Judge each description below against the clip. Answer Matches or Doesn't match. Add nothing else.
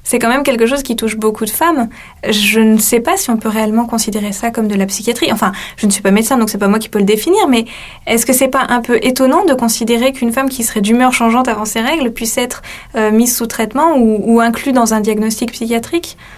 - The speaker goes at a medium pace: Doesn't match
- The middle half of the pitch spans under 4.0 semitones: Matches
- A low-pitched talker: Doesn't match